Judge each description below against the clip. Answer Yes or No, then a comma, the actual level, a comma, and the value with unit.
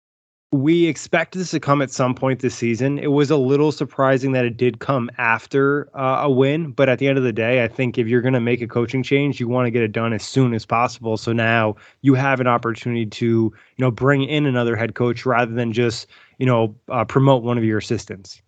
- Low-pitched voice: Yes, low, 125 Hz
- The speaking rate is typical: No, fast, 245 wpm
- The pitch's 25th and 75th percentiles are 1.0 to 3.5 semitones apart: Yes, average, 2.9 semitones